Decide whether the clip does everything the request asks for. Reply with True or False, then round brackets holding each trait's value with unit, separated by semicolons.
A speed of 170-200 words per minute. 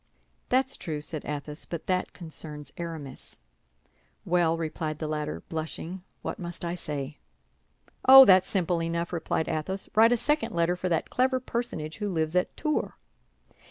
False (155 wpm)